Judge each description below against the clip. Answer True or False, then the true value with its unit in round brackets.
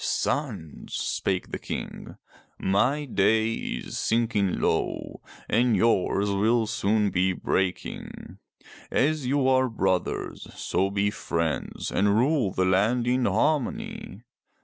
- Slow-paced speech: True (115 wpm)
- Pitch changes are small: False (4.2 semitones)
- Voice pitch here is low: True (105 Hz)